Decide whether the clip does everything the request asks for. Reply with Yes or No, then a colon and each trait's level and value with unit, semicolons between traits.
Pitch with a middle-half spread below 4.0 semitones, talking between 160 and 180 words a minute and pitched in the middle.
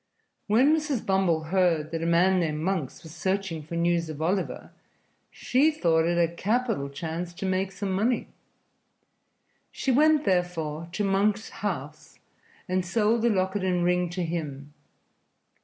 No: average, 3.5 semitones; average, 150 wpm; medium, 180 Hz